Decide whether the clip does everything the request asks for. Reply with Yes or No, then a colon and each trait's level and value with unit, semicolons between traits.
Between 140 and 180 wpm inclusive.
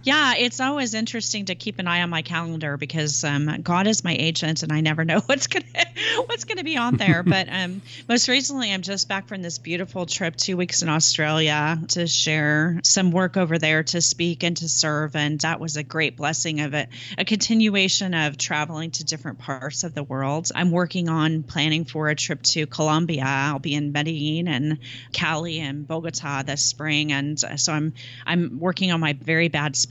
No: average, 200 wpm